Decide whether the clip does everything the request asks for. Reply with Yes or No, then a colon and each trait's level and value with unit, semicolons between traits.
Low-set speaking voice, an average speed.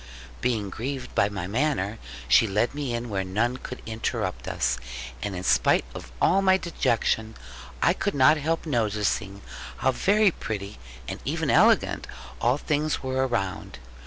Yes: low, 120 Hz; average, 155 wpm